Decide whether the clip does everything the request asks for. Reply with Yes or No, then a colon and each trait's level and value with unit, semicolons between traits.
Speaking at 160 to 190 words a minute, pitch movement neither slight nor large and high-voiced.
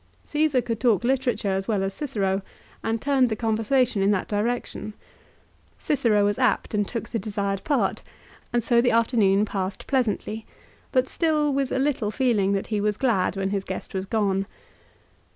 Yes: average, 170 wpm; average, 4.1 semitones; high, 220 Hz